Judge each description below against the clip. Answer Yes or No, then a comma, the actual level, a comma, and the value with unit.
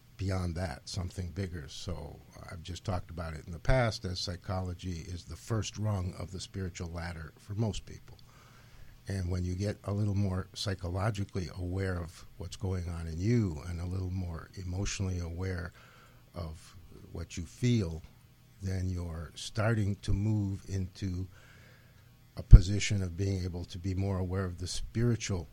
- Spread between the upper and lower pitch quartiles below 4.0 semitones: Yes, average, 3.0 semitones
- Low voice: Yes, very low, 95 Hz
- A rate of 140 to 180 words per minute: Yes, average, 160 wpm